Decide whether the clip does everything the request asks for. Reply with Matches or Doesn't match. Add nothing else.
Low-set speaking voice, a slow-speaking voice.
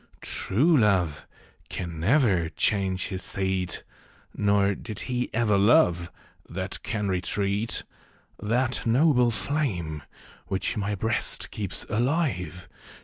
Matches